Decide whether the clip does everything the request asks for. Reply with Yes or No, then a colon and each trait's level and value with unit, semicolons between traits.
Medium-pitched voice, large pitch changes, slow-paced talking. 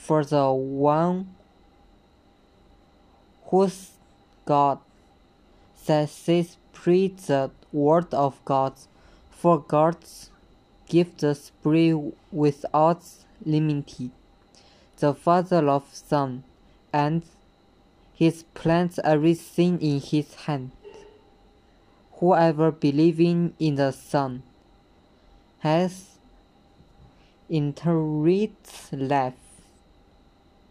No: medium, 155 Hz; average, 3.2 semitones; slow, 70 wpm